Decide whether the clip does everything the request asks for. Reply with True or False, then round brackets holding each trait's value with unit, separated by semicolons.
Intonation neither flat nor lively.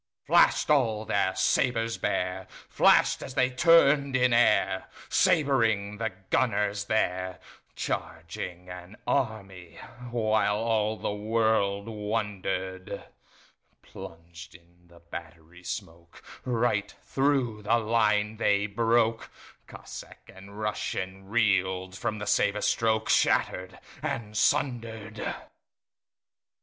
True (3.4 semitones)